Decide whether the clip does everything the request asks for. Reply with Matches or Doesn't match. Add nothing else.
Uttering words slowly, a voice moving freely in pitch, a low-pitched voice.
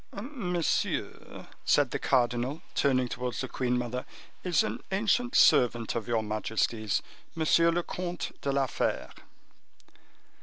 Matches